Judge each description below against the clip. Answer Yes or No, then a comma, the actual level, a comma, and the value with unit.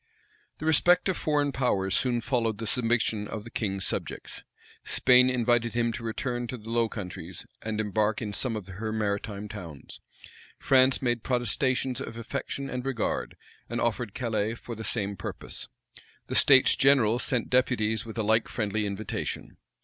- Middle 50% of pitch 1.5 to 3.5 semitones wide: Yes, average, 3.0 semitones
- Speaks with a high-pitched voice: No, low, 115 Hz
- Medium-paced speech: Yes, average, 165 wpm